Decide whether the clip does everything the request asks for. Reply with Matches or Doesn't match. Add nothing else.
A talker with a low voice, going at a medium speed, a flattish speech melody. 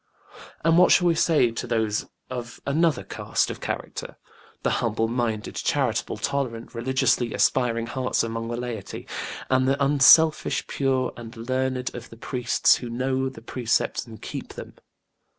Matches